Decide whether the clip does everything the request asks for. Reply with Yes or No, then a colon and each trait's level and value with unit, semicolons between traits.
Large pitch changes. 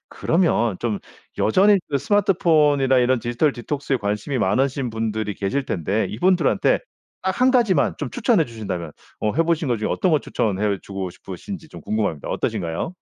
Yes: wide, 7.8 semitones